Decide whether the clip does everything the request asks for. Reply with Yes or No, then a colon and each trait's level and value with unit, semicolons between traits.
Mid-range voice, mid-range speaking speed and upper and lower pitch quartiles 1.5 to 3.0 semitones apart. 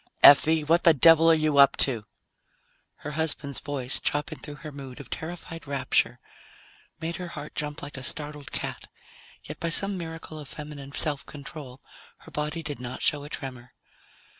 Yes: medium, 150 Hz; average, 175 wpm; narrow, 2.4 semitones